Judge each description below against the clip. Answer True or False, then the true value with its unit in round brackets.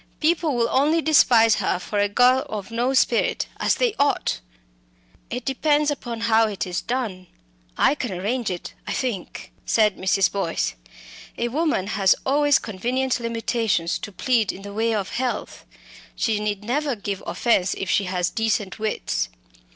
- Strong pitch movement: False (4.4 semitones)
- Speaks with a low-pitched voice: False (230 Hz)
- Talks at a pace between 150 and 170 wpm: True (160 wpm)